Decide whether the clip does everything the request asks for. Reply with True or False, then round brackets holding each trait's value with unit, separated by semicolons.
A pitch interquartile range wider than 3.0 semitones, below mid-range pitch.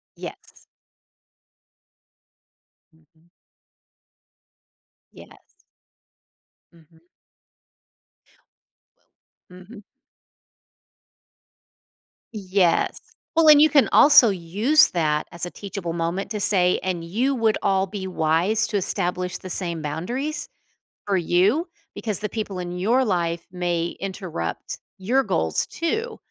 False (4.4 semitones; 190 Hz)